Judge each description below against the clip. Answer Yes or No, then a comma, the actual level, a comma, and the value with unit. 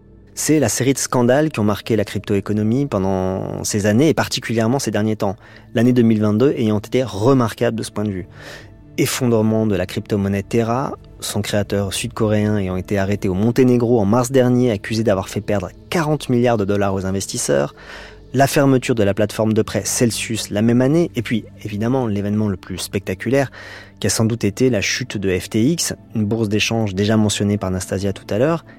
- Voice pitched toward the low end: Yes, low, 110 Hz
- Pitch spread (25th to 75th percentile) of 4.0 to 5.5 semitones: No, average, 3.1 semitones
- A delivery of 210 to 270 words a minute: No, average, 190 wpm